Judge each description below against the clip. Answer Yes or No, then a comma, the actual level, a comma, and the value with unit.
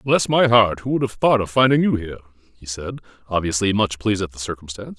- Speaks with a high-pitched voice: No, low, 105 Hz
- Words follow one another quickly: Yes, fast, 230 wpm